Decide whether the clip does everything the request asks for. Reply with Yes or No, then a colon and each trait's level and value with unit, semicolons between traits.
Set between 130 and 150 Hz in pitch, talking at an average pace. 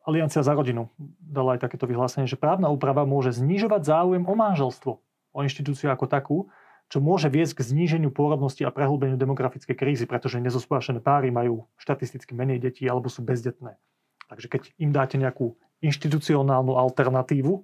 Yes: low, 135 Hz; average, 155 wpm